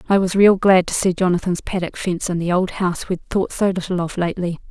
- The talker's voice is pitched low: No, medium, 180 Hz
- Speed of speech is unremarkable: No, fast, 240 wpm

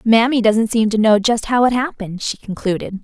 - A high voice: Yes, high, 225 Hz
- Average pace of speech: No, fast, 220 wpm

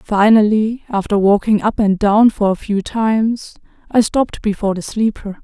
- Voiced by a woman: Yes, female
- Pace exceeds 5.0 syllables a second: No, 4.9 syllables/s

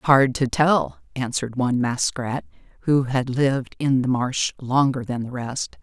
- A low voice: Yes, low, 125 Hz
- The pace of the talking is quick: No, average, 165 wpm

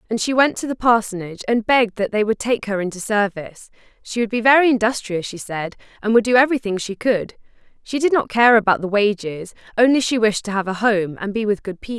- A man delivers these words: No, female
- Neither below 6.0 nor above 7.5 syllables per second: Yes, 6.1 syllables/s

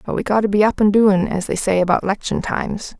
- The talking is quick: Yes, fast, 280 wpm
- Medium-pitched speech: No, high, 205 Hz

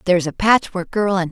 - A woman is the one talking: Yes, female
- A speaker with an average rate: No, fast, 230 wpm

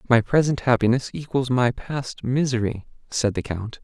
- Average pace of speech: Yes, average, 155 wpm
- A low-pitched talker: Yes, low, 125 Hz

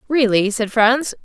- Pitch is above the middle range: Yes, high, 235 Hz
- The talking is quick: No, average, 145 wpm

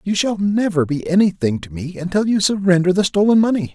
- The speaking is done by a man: Yes, male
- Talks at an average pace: No, fast, 210 wpm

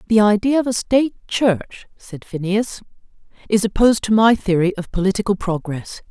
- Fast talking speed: No, average, 155 wpm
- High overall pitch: Yes, high, 210 Hz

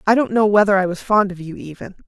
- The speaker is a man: No, female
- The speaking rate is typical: No, fast, 290 wpm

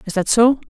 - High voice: Yes, high, 225 Hz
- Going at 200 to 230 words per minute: No, fast, 250 wpm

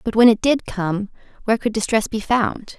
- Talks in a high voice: Yes, high, 220 Hz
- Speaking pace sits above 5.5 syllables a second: No, 5.1 syllables/s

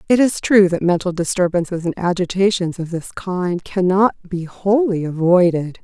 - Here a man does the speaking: No, female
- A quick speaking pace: No, average, 165 wpm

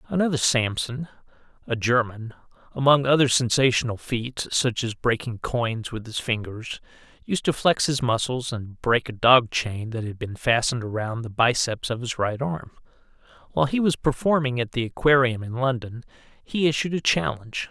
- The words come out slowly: No, average, 165 wpm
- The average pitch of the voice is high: No, low, 125 Hz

